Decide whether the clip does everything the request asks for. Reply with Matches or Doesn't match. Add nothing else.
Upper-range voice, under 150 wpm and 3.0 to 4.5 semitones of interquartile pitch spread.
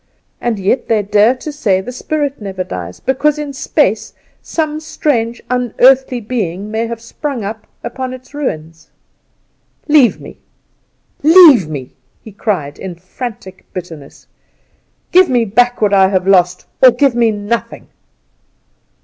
Doesn't match